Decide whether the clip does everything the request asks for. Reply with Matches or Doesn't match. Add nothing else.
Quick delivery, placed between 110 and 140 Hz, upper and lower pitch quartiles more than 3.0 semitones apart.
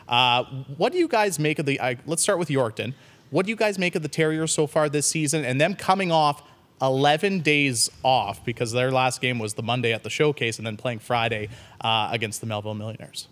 Matches